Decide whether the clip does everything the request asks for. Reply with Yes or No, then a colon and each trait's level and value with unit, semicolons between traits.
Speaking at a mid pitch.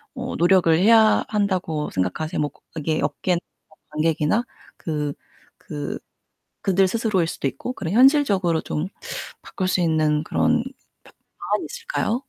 Yes: medium, 175 Hz